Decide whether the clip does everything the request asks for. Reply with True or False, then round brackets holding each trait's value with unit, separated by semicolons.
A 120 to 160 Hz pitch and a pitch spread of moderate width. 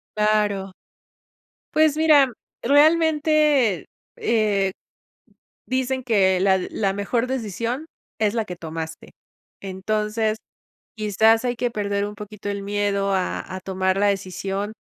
False (210 Hz; 3.8 semitones)